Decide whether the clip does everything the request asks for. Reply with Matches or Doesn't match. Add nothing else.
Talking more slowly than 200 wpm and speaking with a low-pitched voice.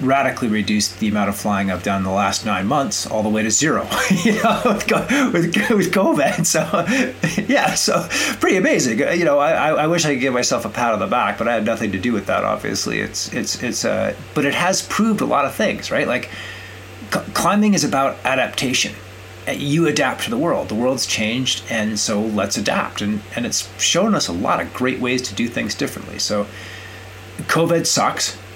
Doesn't match